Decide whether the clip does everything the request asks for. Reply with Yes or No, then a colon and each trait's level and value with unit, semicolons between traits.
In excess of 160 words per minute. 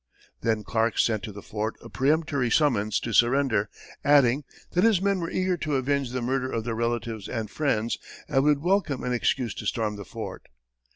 Yes: average, 190 wpm